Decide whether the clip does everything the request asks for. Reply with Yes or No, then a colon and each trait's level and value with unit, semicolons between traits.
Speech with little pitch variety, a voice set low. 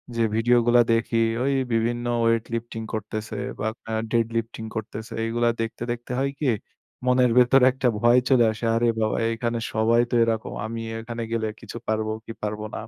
Yes: narrow, 1.2 semitones; low, 115 Hz